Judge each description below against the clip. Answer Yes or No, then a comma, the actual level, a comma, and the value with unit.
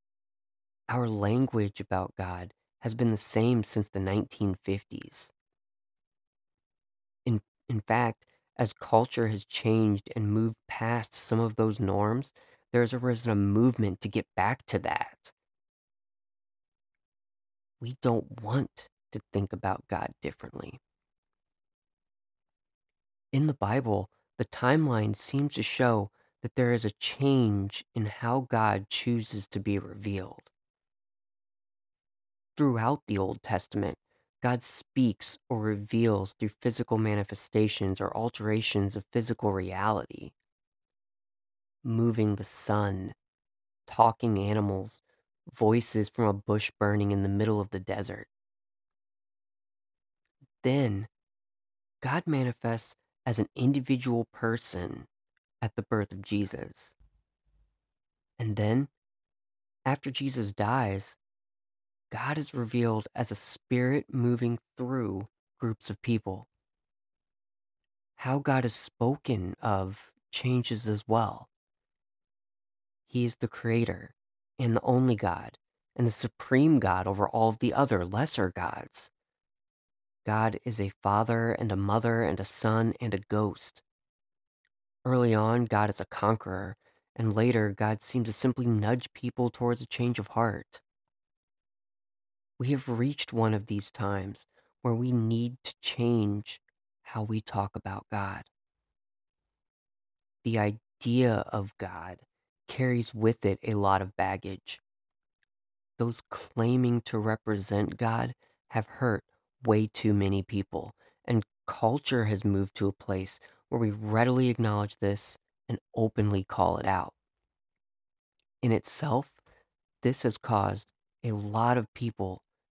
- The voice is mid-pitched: No, low, 110 Hz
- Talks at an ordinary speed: No, slow, 120 wpm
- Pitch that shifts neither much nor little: Yes, average, 3.2 semitones